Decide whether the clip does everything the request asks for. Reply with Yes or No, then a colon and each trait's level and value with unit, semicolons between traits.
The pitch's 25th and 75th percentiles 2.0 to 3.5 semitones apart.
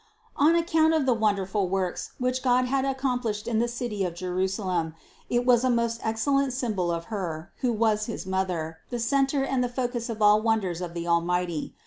No: average, 5.3 semitones